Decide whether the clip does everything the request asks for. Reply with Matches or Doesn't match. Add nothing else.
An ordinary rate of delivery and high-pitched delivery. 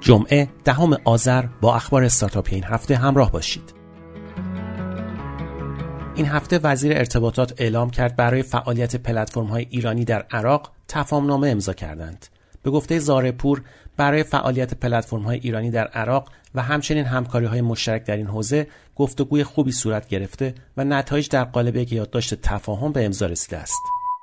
Doesn't match